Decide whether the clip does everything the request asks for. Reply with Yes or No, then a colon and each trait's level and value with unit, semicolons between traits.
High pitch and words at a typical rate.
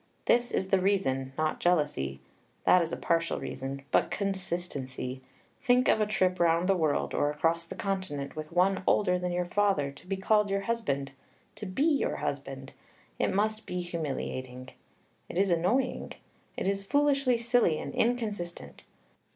No: medium, 180 Hz; average, 160 wpm